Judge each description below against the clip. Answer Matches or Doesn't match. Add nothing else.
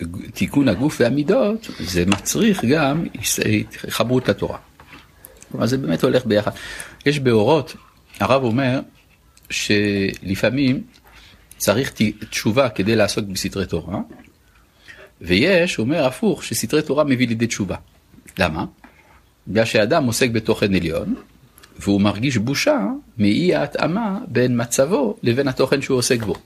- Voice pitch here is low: Matches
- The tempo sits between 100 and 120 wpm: Matches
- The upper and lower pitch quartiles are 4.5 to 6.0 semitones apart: Matches